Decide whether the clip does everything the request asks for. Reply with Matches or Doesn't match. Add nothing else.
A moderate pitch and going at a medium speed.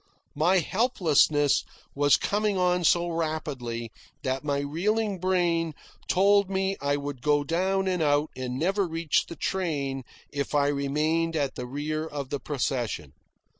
Matches